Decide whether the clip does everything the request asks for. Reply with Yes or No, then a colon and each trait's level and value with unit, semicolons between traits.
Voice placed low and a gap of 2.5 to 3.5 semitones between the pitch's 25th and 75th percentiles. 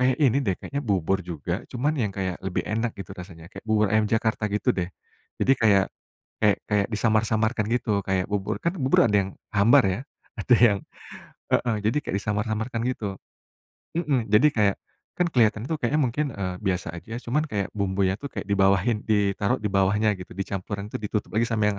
Yes: low, 105 Hz; average, 3.1 semitones